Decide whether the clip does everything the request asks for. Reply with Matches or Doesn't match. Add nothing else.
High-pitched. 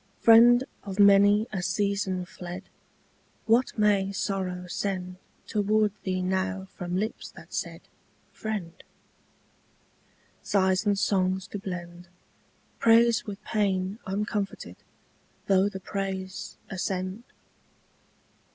Matches